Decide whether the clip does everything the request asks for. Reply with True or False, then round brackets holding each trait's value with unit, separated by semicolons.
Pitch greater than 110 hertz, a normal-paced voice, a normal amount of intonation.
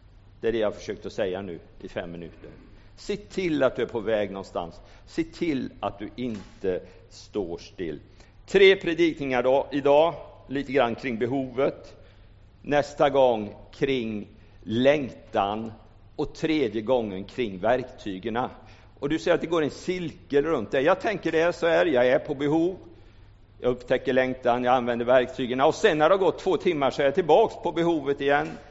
False (130 Hz; 170 wpm; 5.8 semitones)